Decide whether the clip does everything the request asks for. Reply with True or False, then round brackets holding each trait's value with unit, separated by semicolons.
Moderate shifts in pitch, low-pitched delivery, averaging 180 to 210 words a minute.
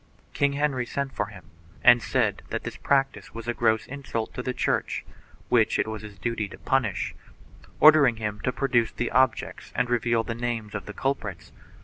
True (3.4 semitones; 120 Hz; 190 wpm)